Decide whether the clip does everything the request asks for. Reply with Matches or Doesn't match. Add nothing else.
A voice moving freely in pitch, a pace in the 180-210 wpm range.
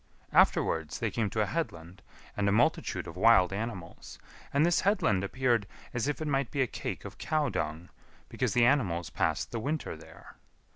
Matches